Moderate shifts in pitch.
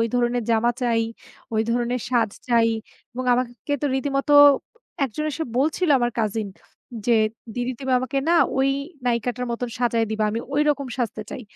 No: narrow, 2.3 semitones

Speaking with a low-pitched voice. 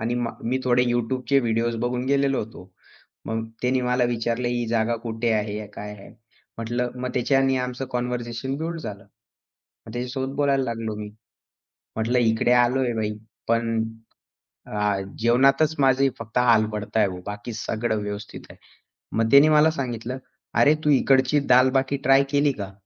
Yes: low, 120 Hz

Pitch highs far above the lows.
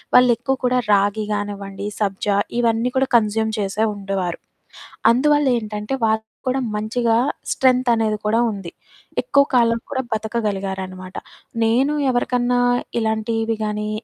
No: average, 3.1 semitones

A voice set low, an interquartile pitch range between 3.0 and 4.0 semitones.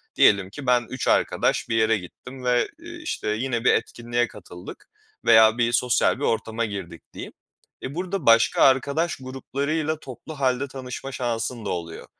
Yes: low, 125 Hz; average, 3.3 semitones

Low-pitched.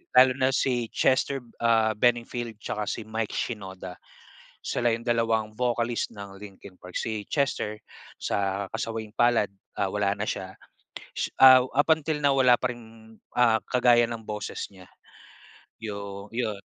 Yes: low, 115 Hz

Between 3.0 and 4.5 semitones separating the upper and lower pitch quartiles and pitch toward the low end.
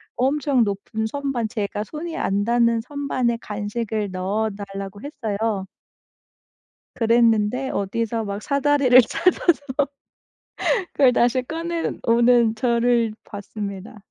No: average, 3.6 semitones; high, 230 Hz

